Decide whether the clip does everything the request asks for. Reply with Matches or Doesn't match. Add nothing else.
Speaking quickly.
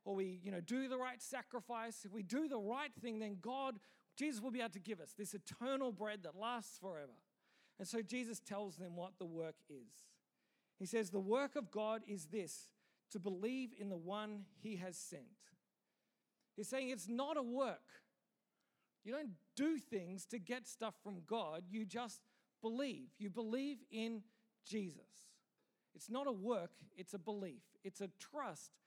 Doesn't match